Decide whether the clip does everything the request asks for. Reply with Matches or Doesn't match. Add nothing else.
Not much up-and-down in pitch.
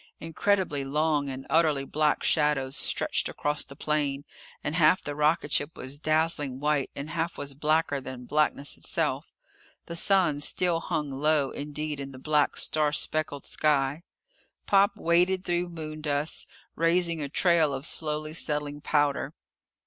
Matches